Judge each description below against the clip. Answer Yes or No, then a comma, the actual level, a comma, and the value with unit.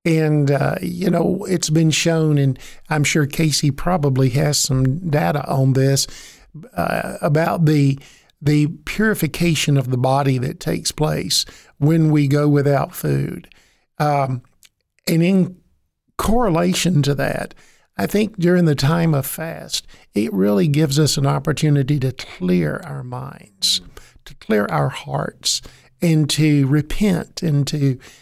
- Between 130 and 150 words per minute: Yes, average, 140 wpm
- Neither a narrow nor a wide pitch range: Yes, average, 3.1 semitones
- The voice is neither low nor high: Yes, medium, 150 Hz